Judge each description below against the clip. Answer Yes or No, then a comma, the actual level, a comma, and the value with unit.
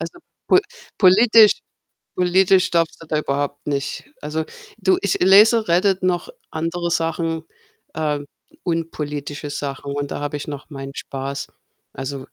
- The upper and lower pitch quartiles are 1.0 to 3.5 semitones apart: No, average, 4.1 semitones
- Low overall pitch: No, medium, 160 Hz